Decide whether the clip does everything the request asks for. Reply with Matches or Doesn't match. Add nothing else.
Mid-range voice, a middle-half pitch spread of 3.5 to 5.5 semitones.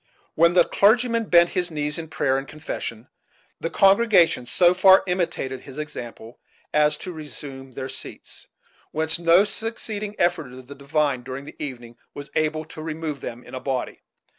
Matches